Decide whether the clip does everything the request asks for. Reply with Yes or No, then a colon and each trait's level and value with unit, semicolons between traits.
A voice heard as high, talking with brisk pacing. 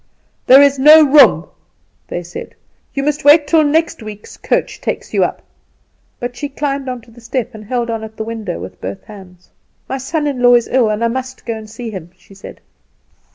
Yes: high, 245 Hz; fast, 210 wpm